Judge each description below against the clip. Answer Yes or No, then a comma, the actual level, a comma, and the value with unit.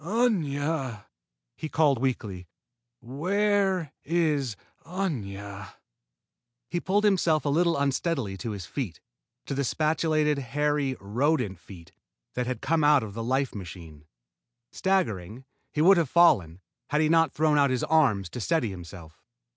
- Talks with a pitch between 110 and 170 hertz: Yes, medium, 140 Hz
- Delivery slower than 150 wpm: Yes, average, 140 wpm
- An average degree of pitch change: No, wide, 7.4 semitones